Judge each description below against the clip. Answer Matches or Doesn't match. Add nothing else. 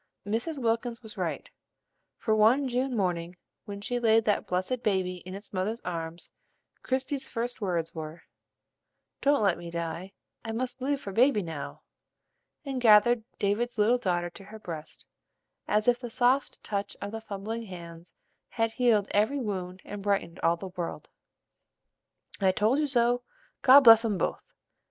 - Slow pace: Doesn't match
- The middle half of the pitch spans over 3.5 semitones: Matches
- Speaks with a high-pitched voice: Matches